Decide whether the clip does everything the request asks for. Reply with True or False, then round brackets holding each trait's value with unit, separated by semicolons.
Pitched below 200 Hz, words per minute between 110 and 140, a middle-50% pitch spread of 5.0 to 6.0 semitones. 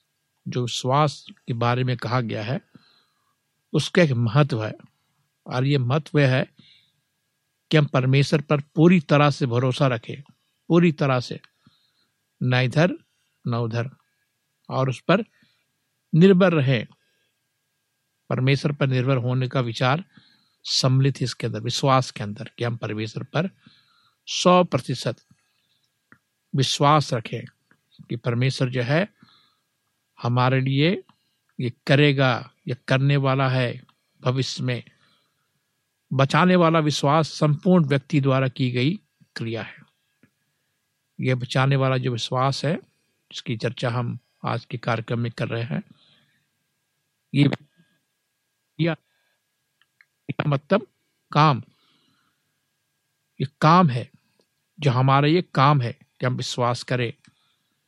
False (135 Hz; 115 wpm; 3.1 semitones)